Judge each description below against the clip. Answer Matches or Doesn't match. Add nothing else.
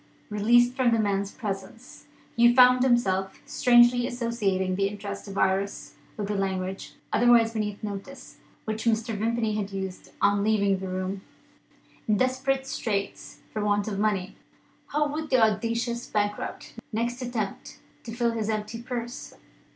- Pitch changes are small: Doesn't match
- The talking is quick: Doesn't match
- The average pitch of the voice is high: Matches